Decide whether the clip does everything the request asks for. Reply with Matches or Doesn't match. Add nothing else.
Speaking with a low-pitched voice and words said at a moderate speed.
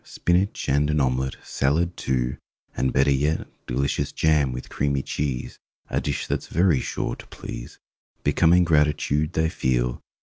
Matches